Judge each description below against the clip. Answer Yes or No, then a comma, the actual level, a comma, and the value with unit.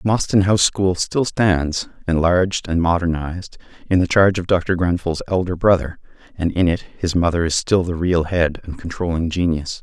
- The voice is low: Yes, very low, 90 Hz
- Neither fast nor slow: Yes, average, 175 wpm